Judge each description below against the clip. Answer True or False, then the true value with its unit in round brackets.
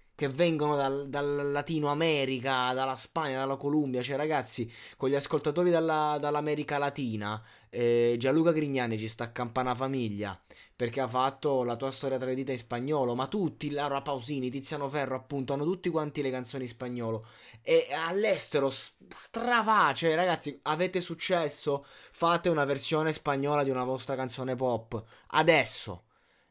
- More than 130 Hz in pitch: True (140 Hz)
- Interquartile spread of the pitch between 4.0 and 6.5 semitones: False (3.0 semitones)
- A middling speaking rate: True (145 wpm)